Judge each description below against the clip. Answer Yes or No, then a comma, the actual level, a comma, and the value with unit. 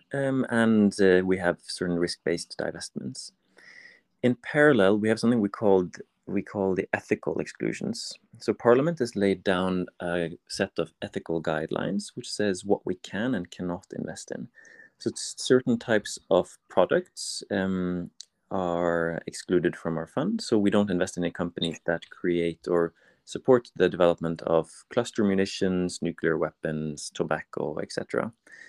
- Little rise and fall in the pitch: No, average, 3.6 semitones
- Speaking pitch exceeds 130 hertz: No, very low, 95 Hz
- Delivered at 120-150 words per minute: Yes, average, 145 wpm